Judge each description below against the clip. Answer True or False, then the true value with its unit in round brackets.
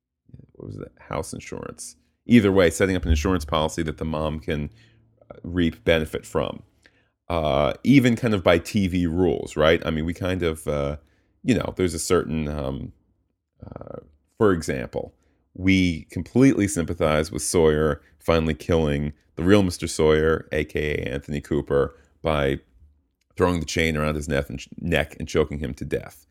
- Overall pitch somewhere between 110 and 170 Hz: False (80 Hz)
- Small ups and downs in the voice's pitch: False (3.1 semitones)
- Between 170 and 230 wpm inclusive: False (155 wpm)